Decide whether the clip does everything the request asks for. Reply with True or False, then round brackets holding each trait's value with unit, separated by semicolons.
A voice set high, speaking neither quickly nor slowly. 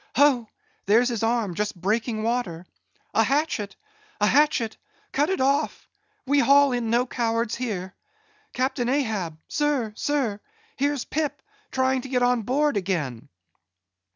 False (245 Hz; 130 wpm)